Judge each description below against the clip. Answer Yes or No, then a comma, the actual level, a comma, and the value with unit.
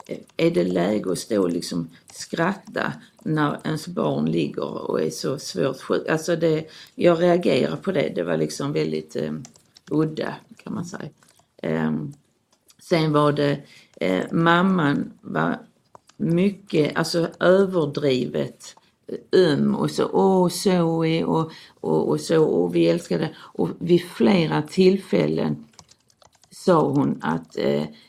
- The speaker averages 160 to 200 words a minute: No, average, 130 wpm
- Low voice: No, medium, 160 Hz